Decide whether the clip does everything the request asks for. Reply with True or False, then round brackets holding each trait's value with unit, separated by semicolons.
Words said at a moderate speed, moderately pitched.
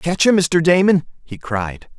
True (180 wpm; 160 Hz)